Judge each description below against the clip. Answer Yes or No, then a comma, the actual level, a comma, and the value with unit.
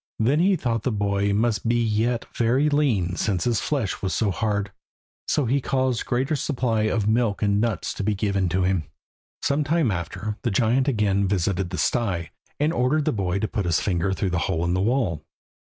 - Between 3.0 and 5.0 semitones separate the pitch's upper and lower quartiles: Yes, average, 4.2 semitones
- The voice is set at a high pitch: No, low, 110 Hz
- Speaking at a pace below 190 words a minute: No, fast, 205 wpm